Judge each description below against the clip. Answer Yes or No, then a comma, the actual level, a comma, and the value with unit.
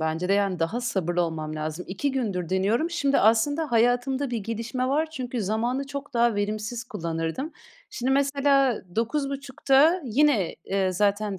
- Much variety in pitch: Yes, wide, 6.0 semitones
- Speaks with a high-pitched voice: Yes, high, 235 Hz